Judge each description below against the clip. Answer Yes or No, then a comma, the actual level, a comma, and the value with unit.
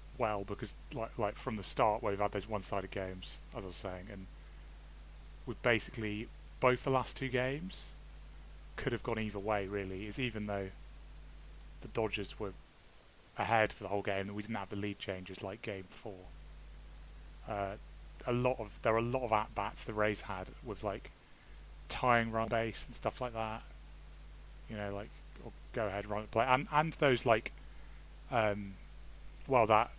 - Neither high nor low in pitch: No, low, 105 Hz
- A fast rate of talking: No, average, 180 wpm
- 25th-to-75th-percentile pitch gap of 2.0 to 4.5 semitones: Yes, average, 3.3 semitones